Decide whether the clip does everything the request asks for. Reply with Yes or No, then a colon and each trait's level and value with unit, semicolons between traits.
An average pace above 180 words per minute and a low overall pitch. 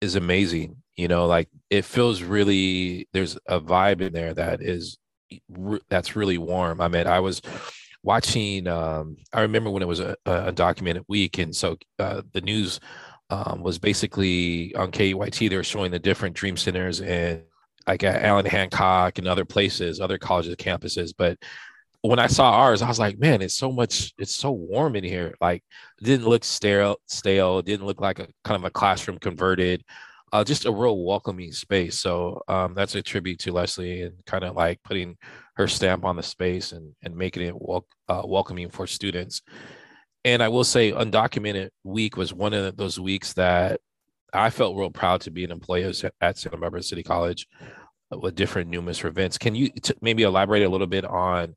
Yes: average, 190 wpm; very low, 95 Hz